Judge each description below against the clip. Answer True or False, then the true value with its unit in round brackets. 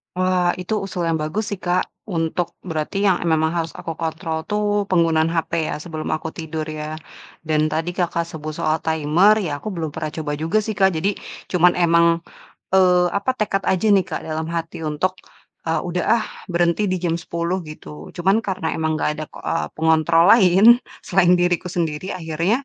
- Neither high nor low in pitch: True (170 Hz)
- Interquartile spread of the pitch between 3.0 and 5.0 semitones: False (2.4 semitones)